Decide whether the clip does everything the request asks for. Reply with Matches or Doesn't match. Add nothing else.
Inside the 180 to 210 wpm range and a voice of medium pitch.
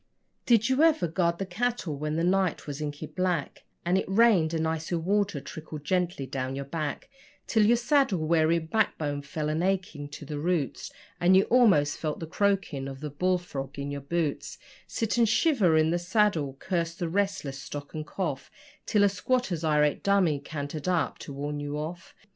Matches